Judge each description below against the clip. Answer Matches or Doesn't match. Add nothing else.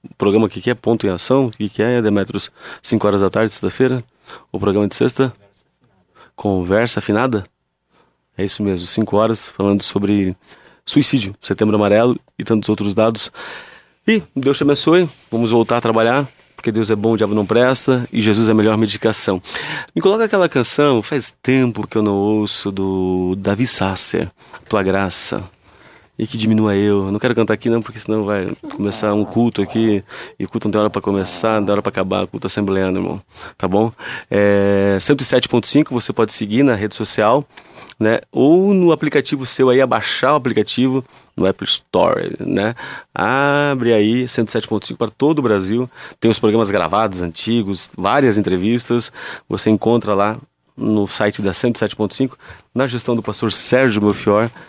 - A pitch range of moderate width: Matches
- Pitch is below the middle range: Matches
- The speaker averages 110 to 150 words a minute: Doesn't match